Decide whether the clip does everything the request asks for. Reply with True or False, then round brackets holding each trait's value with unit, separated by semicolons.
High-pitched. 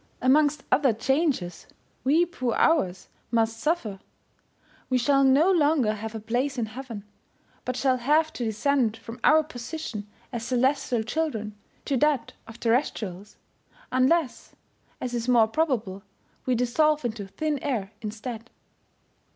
True (250 Hz)